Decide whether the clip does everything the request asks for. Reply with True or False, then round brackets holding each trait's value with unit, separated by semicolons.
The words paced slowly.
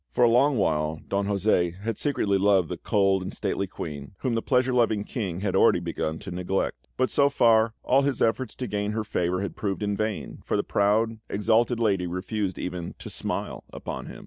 False (205 wpm)